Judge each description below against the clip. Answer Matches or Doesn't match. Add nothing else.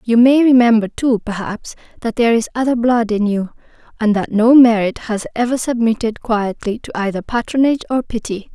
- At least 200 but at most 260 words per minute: Doesn't match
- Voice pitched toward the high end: Matches